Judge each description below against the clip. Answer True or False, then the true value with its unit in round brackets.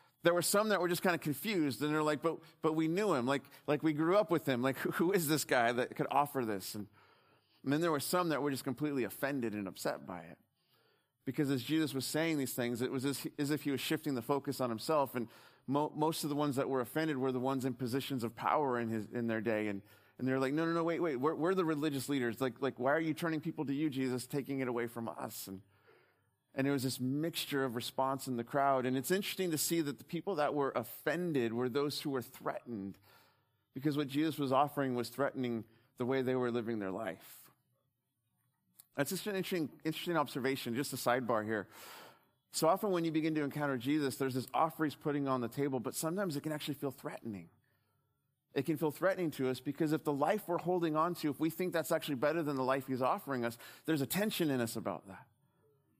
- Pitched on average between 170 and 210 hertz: False (140 Hz)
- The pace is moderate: False (240 wpm)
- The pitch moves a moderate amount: True (3.7 semitones)